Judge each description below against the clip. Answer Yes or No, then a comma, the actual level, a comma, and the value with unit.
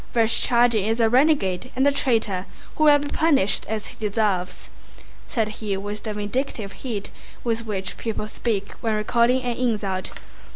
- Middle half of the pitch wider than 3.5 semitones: No, average, 3.2 semitones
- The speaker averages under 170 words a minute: Yes, average, 160 wpm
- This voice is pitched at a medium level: No, high, 220 Hz